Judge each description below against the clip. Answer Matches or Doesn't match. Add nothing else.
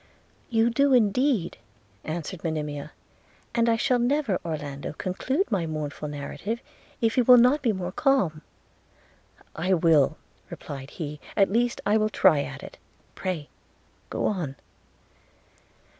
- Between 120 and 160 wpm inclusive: Matches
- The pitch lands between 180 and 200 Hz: Matches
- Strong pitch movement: Matches